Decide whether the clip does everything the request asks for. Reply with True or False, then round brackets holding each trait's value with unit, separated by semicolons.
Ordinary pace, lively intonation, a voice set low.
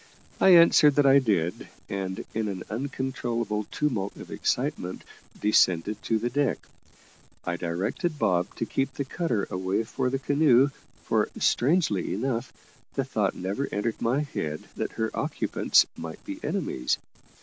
True (145 wpm; 6.0 semitones; 115 Hz)